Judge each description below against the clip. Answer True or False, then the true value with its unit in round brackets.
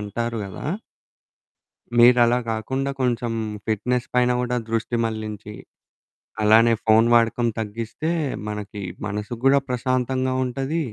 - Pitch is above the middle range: False (120 Hz)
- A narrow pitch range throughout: True (2.3 semitones)